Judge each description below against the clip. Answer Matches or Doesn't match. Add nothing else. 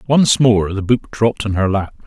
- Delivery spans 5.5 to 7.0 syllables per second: Doesn't match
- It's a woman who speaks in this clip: Doesn't match